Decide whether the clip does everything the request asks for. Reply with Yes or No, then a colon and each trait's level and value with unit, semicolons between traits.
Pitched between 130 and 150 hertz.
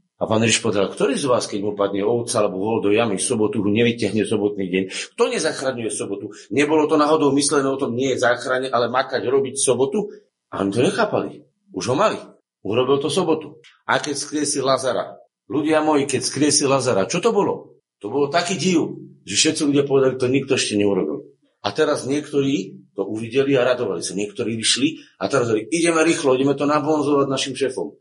Yes: low, 135 Hz